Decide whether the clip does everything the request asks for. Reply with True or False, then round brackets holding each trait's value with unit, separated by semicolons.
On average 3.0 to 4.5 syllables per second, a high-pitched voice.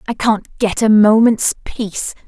True (4.1 syllables/s; 215 Hz)